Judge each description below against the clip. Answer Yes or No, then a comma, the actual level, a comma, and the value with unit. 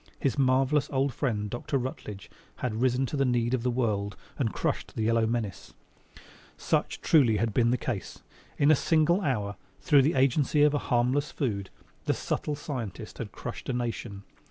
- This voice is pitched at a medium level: No, low, 125 Hz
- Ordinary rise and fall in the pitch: Yes, average, 3.7 semitones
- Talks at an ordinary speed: Yes, average, 180 wpm